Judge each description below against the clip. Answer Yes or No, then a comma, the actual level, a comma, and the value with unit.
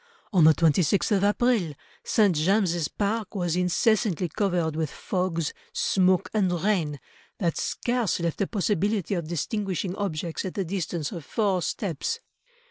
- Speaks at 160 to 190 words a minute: No, average, 140 wpm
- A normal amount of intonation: Yes, average, 3.6 semitones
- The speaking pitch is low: No, medium, 185 Hz